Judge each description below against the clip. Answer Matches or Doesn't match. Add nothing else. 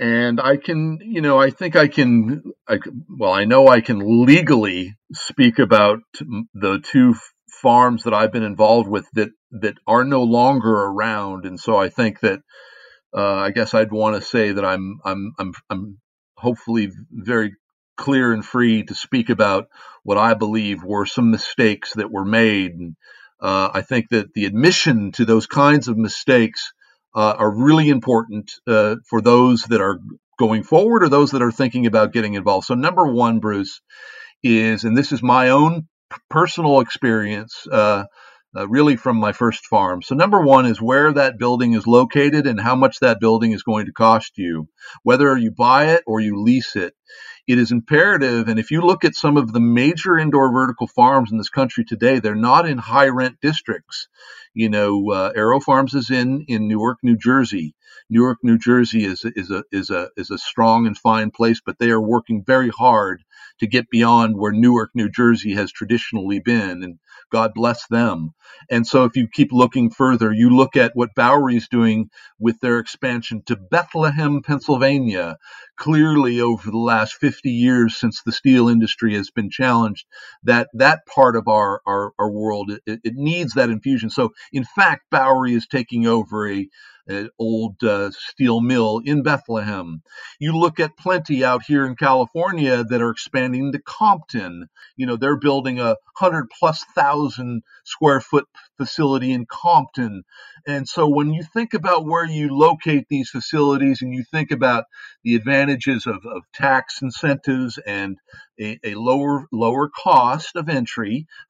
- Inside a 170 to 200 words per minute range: Matches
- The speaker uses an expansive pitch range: Doesn't match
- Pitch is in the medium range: Doesn't match